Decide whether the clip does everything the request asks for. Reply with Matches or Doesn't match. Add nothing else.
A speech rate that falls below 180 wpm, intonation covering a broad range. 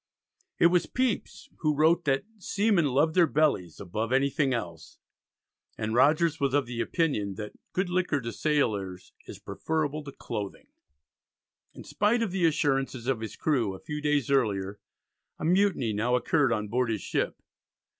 Matches